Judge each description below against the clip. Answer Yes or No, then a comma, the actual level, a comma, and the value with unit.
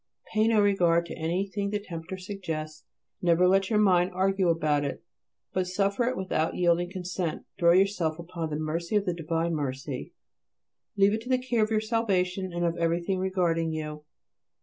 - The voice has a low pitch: No, medium, 180 Hz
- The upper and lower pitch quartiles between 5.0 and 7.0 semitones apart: No, average, 3.1 semitones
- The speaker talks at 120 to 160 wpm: No, average, 175 wpm